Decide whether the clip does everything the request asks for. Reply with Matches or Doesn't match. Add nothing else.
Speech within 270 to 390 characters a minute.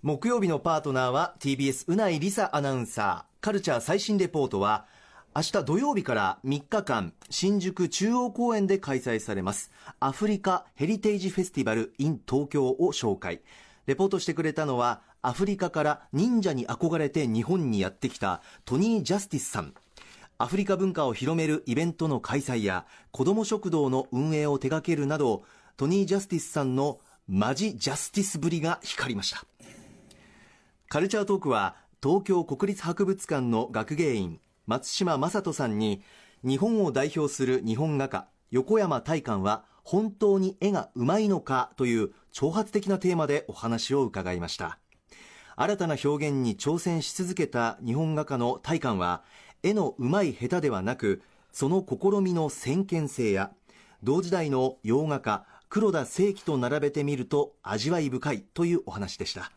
Matches